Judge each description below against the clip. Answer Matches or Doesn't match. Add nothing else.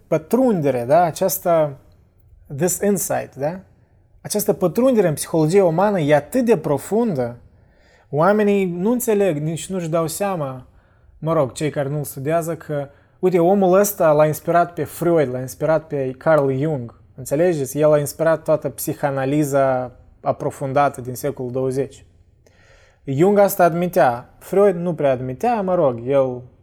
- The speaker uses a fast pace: Doesn't match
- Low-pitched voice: Doesn't match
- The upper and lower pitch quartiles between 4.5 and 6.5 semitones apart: Matches